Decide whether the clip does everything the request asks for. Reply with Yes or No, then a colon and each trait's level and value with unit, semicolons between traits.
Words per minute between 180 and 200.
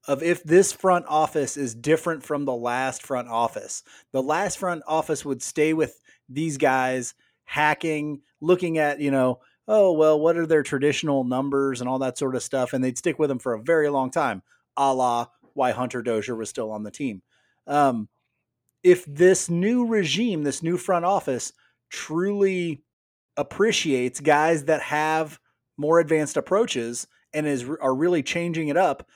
No: average, 170 wpm